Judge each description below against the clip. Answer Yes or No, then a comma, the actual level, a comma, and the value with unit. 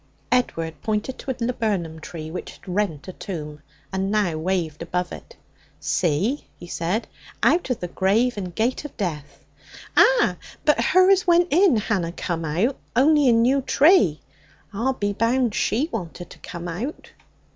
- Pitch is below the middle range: No, high, 205 Hz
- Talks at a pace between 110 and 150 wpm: No, average, 170 wpm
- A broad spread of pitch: Yes, wide, 6.8 semitones